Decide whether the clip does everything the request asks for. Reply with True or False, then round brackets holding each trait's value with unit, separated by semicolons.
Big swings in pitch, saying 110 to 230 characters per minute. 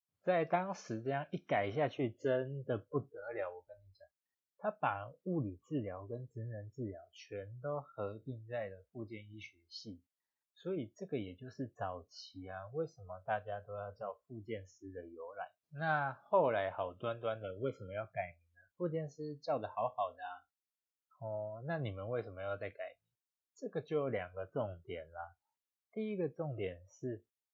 False (6.2 semitones; 245 characters per minute)